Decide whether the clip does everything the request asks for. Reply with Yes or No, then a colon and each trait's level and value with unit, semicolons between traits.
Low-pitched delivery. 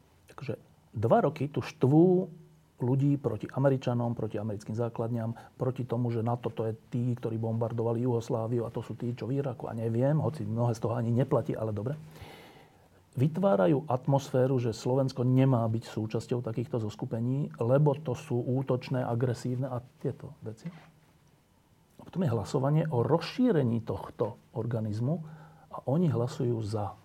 Yes: low, 125 Hz